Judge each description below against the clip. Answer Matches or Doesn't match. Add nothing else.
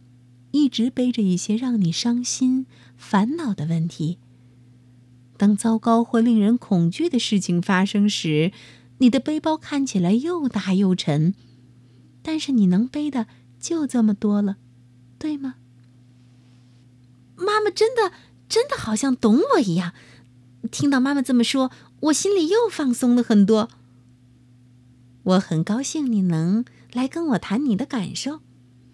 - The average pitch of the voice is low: Doesn't match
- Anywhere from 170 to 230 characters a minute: Matches